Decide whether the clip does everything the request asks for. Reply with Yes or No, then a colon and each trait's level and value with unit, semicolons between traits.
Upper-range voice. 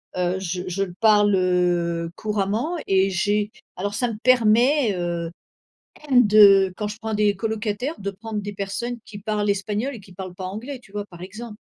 Yes: high, 205 Hz